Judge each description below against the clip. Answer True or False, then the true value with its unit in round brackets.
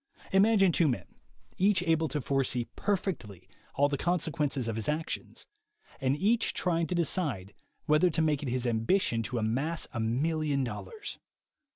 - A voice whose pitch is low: False (150 Hz)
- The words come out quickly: False (155 wpm)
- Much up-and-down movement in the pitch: True (5.8 semitones)